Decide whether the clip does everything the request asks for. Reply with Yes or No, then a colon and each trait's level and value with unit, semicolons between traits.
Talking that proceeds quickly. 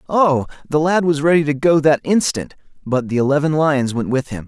Yes: fast, 215 wpm